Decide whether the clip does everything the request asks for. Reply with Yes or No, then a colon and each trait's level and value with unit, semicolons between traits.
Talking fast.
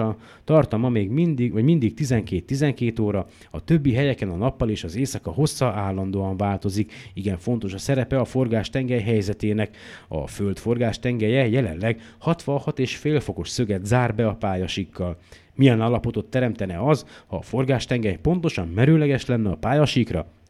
No: average, 145 wpm